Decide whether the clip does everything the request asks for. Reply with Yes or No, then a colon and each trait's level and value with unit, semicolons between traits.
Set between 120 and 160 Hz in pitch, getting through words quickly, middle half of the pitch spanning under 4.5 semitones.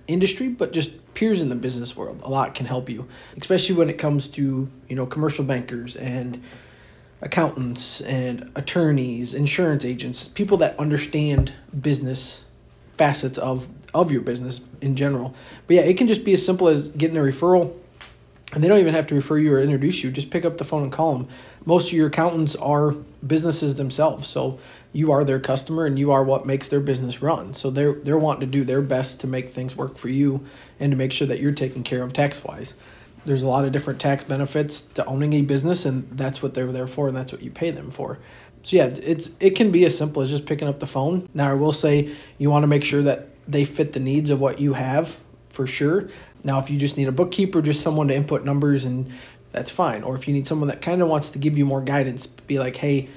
Yes: medium, 140 Hz; fast, 230 wpm; average, 2.8 semitones